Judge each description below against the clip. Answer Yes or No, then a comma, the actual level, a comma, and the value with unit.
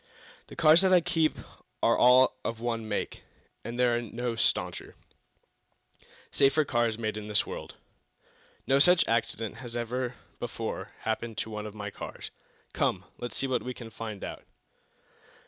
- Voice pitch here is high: No, low, 120 Hz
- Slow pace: No, average, 160 wpm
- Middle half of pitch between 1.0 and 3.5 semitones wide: Yes, average, 2.7 semitones